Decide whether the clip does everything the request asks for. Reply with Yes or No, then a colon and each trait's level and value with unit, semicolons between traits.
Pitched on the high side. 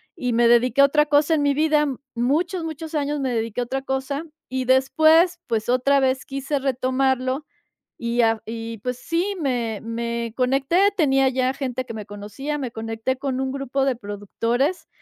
Yes: very high, 265 Hz